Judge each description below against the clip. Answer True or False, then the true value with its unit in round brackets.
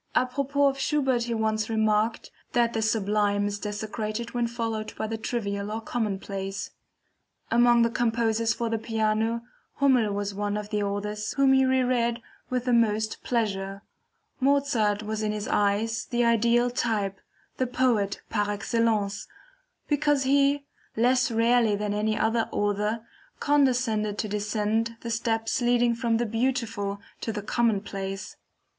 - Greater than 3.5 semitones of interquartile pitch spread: False (2.4 semitones)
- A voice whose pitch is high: True (225 Hz)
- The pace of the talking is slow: False (145 wpm)